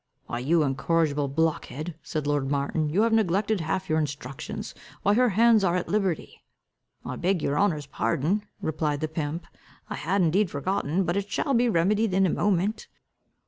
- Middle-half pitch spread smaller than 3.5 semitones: No, average, 5.1 semitones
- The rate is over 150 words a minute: Yes, average, 175 wpm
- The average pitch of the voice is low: No, medium, 170 Hz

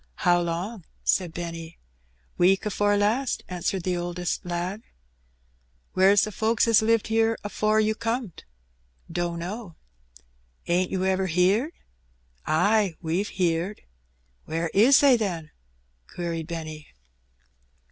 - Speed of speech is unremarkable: No, slow, 115 wpm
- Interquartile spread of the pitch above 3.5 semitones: Yes, average, 4.0 semitones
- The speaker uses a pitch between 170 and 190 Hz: Yes, medium, 185 Hz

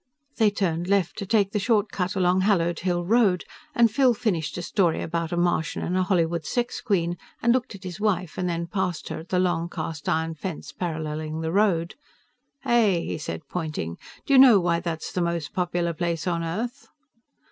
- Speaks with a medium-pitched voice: Yes, medium, 175 Hz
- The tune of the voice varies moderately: Yes, average, 3.2 semitones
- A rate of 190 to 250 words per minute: Yes, average, 200 wpm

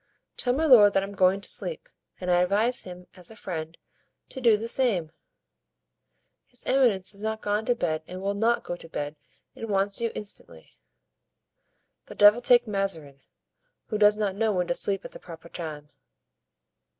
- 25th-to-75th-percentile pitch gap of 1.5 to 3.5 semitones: No, average, 3.9 semitones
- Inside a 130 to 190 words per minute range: Yes, average, 180 wpm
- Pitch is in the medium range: No, high, 200 Hz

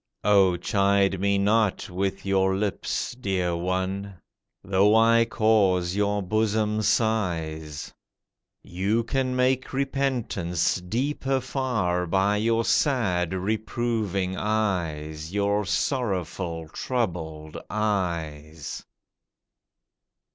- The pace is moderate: No, slow, 90 wpm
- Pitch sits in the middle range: No, low, 100 Hz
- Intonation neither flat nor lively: Yes, average, 3.8 semitones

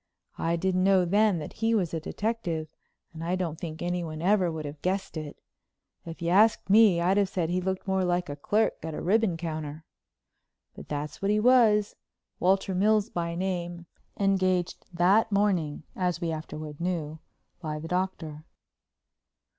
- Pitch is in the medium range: Yes, medium, 180 Hz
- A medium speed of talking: Yes, average, 170 wpm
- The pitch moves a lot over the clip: No, average, 3.3 semitones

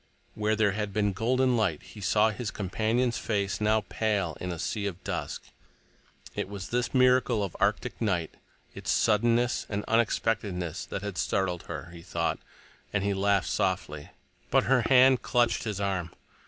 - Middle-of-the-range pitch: No, low, 105 Hz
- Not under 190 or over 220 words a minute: No, average, 165 wpm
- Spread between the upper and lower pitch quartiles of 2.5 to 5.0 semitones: Yes, average, 3.2 semitones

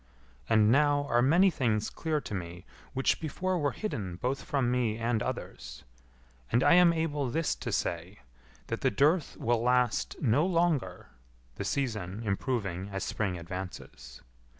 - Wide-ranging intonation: Yes, wide, 6.6 semitones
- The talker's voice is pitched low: Yes, low, 120 Hz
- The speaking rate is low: No, average, 150 wpm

